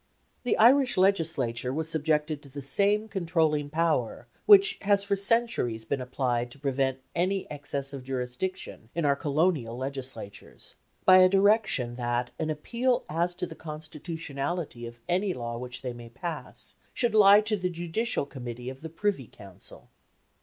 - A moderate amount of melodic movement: No, wide, 6.5 semitones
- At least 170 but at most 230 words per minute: No, average, 155 wpm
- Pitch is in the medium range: Yes, medium, 155 Hz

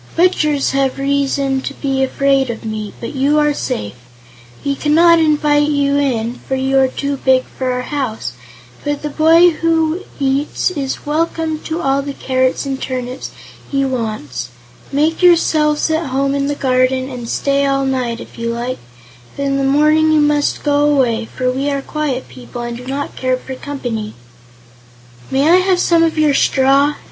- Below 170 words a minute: No, average, 175 wpm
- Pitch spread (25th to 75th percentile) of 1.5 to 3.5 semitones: Yes, narrow, 2.6 semitones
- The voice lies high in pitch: Yes, very high, 275 Hz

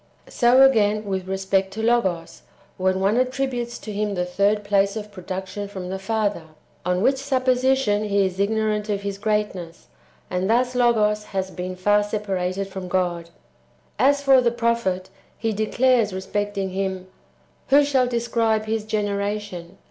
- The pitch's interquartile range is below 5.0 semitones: Yes, average, 3.5 semitones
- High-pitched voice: Yes, high, 205 Hz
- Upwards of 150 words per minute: Yes, average, 160 wpm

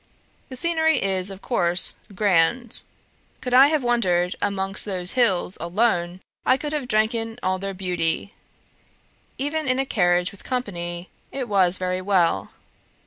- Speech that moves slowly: No, average, 150 wpm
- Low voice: No, high, 195 Hz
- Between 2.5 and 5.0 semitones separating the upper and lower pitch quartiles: No, wide, 5.6 semitones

